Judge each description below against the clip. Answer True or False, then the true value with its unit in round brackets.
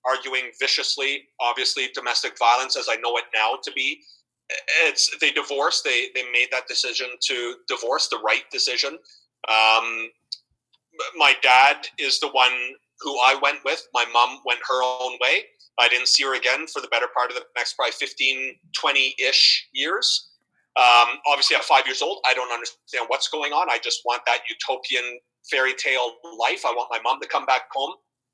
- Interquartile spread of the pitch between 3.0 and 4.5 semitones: True (3.3 semitones)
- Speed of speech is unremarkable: True (180 wpm)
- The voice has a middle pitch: False (125 Hz)